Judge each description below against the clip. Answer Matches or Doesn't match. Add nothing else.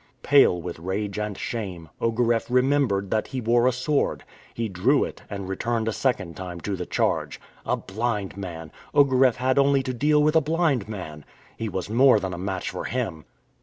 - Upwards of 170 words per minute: Matches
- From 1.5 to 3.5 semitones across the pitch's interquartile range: Doesn't match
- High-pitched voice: Doesn't match